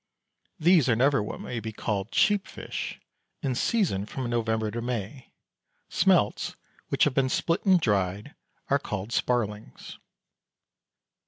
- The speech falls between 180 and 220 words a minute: No, slow, 135 wpm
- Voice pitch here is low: Yes, low, 120 Hz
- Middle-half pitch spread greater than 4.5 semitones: Yes, average, 4.9 semitones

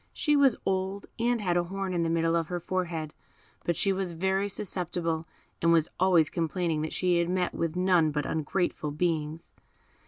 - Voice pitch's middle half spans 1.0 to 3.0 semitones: Yes, narrow, 2.6 semitones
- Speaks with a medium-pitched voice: Yes, medium, 175 Hz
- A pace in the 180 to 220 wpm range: Yes, average, 185 wpm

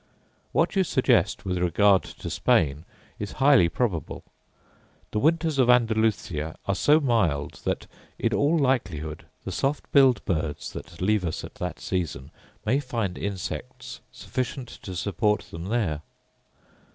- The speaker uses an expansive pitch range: Yes, wide, 7.2 semitones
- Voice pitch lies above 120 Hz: No, low, 105 Hz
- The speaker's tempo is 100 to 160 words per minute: Yes, average, 140 wpm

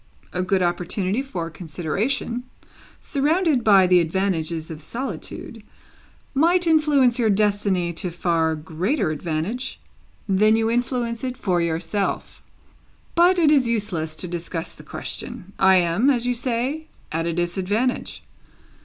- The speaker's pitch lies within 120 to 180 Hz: No, high, 200 Hz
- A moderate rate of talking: No, slow, 130 wpm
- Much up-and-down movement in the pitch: Yes, wide, 6.4 semitones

